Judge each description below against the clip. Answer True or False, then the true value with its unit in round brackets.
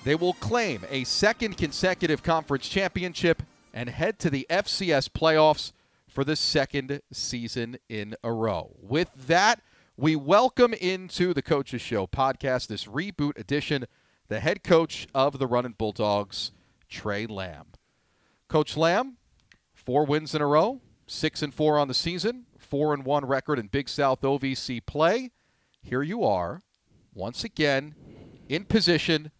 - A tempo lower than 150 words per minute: True (140 wpm)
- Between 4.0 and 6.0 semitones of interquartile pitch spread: True (5.1 semitones)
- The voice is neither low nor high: True (145 Hz)